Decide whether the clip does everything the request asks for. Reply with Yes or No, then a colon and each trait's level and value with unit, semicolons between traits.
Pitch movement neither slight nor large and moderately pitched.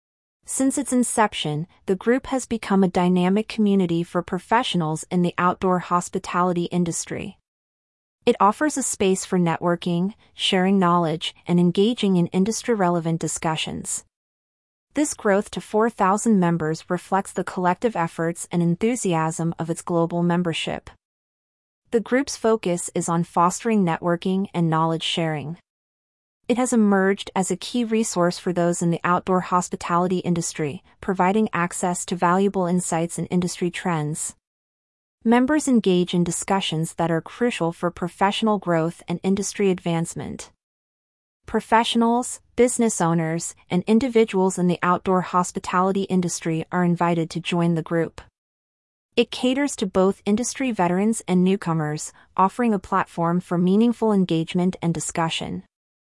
Yes: average, 3.3 semitones; medium, 180 Hz